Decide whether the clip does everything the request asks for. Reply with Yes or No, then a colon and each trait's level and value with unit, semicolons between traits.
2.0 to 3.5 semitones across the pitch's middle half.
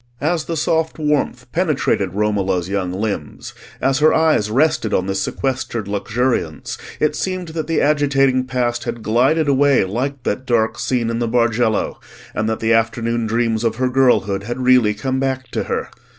No: average, 4.1 semitones